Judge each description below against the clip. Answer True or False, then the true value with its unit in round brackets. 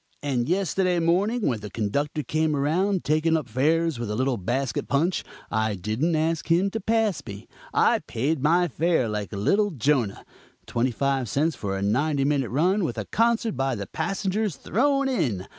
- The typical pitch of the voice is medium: True (150 Hz)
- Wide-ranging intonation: True (6.8 semitones)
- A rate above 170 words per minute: True (180 wpm)